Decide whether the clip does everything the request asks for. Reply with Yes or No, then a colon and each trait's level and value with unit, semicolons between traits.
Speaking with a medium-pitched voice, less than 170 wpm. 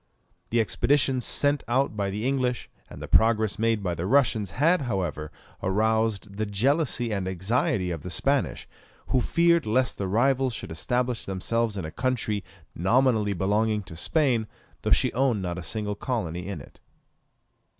No: low, 110 Hz; average, 160 wpm